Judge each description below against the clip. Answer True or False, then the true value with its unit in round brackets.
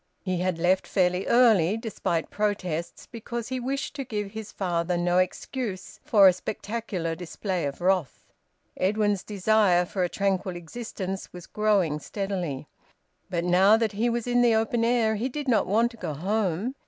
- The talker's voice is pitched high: True (195 Hz)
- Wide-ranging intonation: False (3.9 semitones)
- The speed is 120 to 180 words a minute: True (165 wpm)